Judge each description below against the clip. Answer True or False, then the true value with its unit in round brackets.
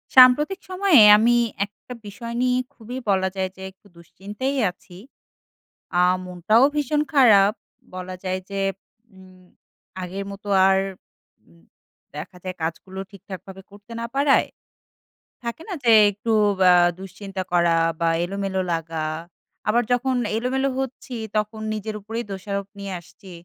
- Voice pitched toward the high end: True (200 Hz)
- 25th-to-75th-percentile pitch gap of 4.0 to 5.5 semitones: True (4.3 semitones)